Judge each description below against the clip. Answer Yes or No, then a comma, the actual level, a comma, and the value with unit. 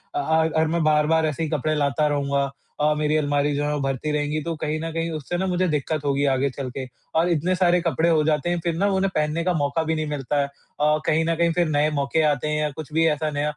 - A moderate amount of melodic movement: No, narrow, 2.0 semitones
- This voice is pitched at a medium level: Yes, medium, 155 Hz